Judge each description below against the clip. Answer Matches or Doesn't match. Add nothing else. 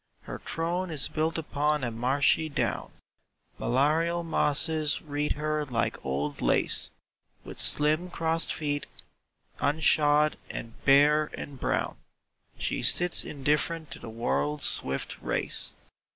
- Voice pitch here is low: Doesn't match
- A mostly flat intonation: Matches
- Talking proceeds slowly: Matches